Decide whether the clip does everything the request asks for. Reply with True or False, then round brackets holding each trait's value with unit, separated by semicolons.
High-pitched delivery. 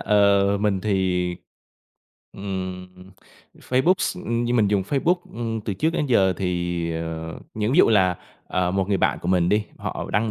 False (100 Hz)